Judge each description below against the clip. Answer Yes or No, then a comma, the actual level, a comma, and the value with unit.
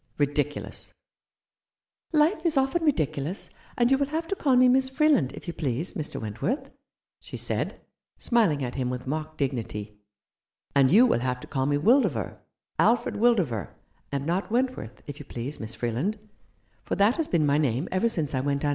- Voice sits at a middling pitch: Yes, medium, 155 Hz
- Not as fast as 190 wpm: No, average, 200 wpm